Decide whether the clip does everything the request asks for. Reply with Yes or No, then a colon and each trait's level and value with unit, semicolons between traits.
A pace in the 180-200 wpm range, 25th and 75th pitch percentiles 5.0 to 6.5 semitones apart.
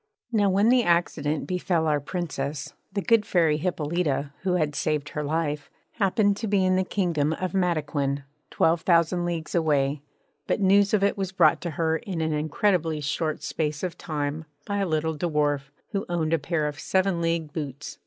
No: average, 185 wpm; average, 3.8 semitones